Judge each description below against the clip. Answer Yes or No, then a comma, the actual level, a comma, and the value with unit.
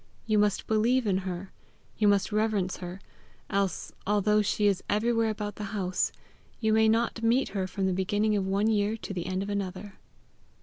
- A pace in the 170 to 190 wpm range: Yes, average, 185 wpm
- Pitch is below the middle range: No, high, 205 Hz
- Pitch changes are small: Yes, narrow, 2.2 semitones